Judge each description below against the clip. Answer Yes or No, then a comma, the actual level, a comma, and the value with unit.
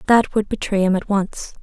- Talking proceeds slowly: No, fast, 220 wpm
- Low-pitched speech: No, high, 200 Hz